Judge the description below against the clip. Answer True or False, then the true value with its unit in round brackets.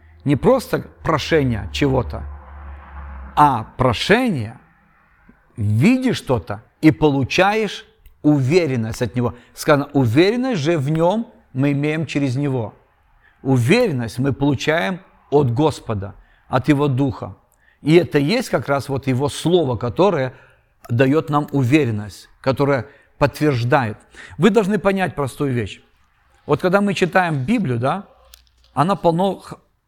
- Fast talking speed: False (115 wpm)